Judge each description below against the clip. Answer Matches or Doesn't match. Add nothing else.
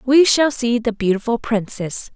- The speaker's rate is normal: Matches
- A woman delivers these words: Matches